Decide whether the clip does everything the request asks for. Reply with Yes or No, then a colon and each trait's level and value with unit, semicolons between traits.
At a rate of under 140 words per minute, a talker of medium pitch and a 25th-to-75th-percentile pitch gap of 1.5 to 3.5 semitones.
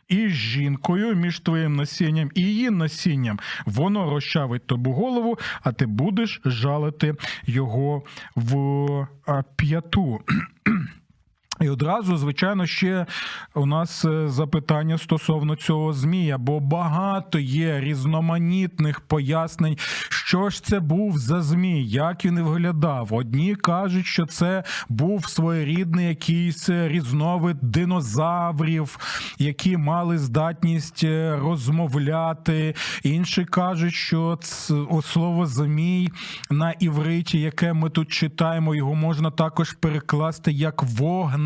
Yes: average, 110 wpm; medium, 160 Hz; average, 2.8 semitones